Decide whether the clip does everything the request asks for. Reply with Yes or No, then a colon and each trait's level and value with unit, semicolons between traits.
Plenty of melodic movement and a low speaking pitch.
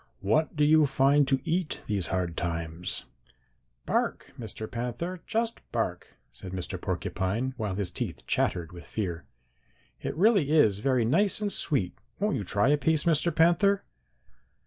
Yes: wide, 8.7 semitones; low, 130 Hz